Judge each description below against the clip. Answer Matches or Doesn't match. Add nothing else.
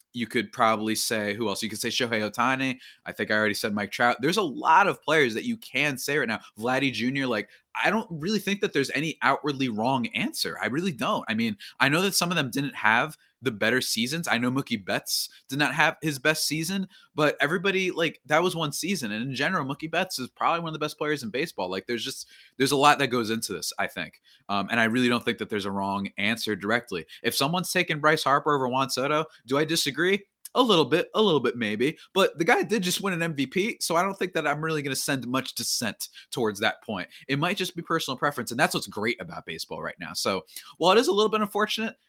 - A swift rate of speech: Matches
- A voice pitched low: Doesn't match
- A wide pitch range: Matches